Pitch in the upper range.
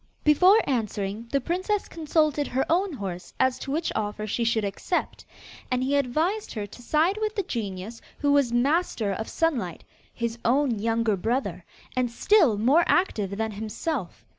Yes: very high, 250 Hz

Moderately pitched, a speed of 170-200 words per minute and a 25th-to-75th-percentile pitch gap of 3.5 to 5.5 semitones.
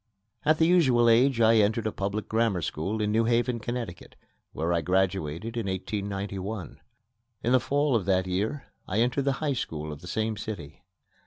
No: low, 110 Hz; average, 180 wpm; average, 4.1 semitones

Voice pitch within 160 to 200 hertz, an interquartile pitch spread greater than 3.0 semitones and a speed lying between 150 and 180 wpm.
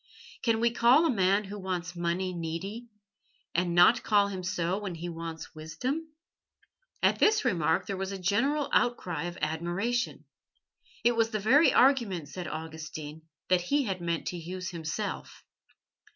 Yes: medium, 185 Hz; average, 5.1 semitones; average, 155 wpm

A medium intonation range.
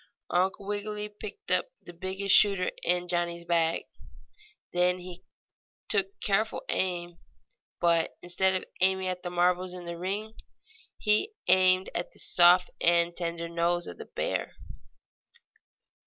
No: narrow, 1.8 semitones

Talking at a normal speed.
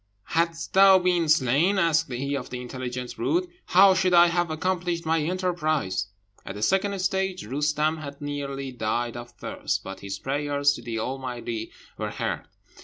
Yes: average, 165 wpm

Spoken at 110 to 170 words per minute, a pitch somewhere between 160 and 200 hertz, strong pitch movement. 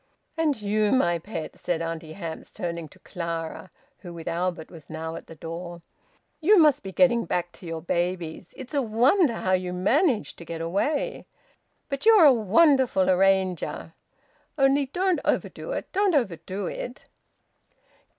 Yes: average, 155 wpm; high, 190 Hz; wide, 8.2 semitones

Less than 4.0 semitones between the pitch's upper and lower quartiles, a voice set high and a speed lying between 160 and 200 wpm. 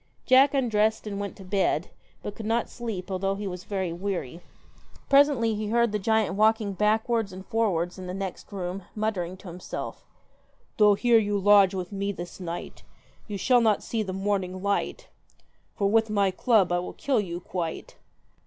Yes: average, 2.9 semitones; high, 200 Hz; average, 180 wpm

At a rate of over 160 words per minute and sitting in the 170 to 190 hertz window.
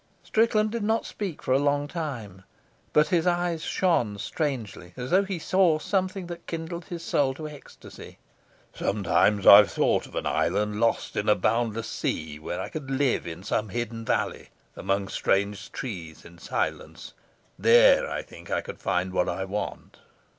No: average, 170 wpm; low, 135 Hz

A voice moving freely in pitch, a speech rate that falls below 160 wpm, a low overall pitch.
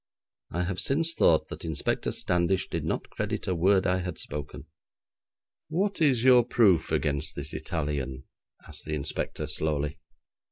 Yes: wide, 7.0 semitones; average, 150 wpm; very low, 85 Hz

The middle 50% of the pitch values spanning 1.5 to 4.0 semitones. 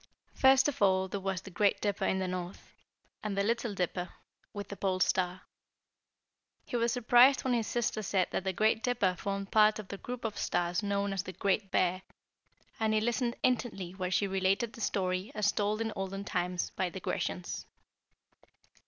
Yes: average, 2.8 semitones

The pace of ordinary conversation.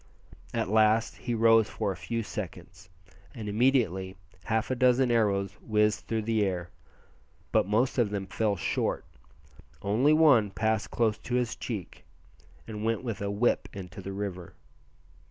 Yes: average, 155 wpm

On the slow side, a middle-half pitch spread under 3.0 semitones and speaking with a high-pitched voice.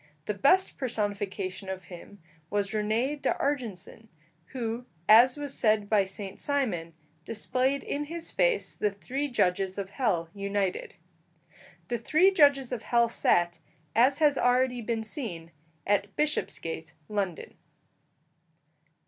No: slow, 125 wpm; average, 5.2 semitones; high, 220 Hz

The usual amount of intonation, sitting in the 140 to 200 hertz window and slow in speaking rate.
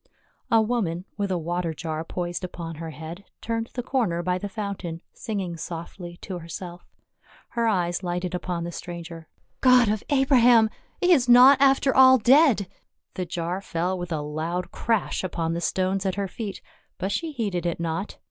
No: average, 4.9 semitones; medium, 185 Hz; average, 180 wpm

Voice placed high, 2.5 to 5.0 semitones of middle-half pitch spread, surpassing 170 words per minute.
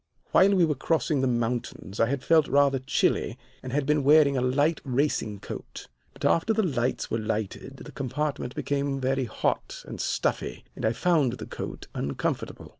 No: low, 135 Hz; average, 3.4 semitones; average, 180 wpm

